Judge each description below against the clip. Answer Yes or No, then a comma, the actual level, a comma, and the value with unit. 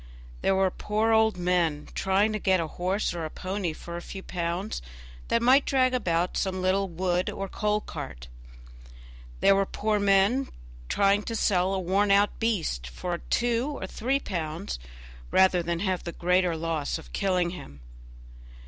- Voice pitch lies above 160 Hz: Yes, high, 190 Hz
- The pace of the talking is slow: No, average, 165 wpm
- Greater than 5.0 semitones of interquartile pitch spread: No, average, 3.3 semitones